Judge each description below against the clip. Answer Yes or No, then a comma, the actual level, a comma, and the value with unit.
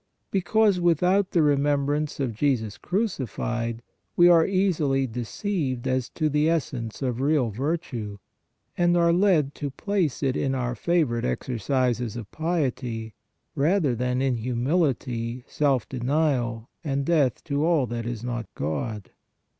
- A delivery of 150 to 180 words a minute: No, average, 140 wpm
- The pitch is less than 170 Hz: Yes, low, 135 Hz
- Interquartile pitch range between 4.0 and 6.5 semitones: Yes, average, 5.2 semitones